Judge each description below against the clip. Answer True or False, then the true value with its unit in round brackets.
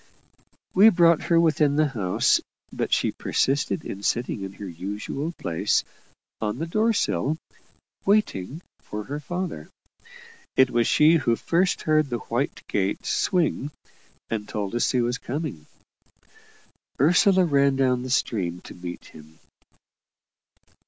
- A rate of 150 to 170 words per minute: False (140 wpm)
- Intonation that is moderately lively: False (7.8 semitones)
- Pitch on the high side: False (135 Hz)